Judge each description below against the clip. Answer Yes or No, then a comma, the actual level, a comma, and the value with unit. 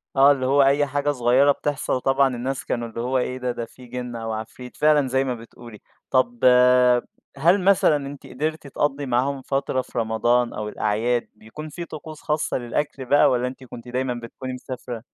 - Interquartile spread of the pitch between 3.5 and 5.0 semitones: No, average, 2.7 semitones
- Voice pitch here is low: Yes, low, 130 Hz